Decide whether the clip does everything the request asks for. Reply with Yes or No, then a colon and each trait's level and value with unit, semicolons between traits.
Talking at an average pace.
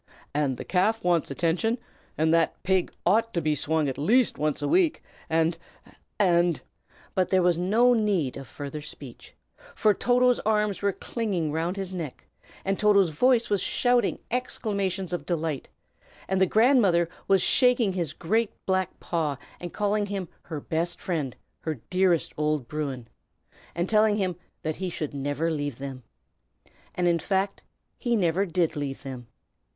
Yes: average, 160 wpm